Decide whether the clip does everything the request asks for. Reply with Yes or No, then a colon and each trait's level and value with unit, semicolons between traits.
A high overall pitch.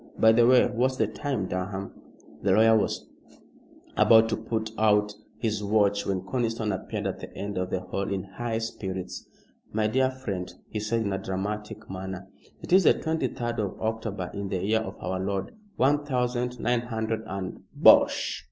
No: low, 110 Hz